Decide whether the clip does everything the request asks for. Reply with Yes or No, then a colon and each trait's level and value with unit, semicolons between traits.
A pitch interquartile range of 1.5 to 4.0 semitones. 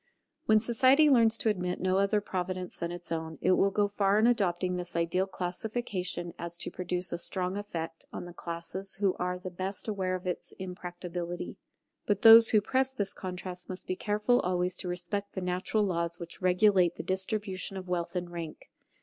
Yes: narrow, 2.5 semitones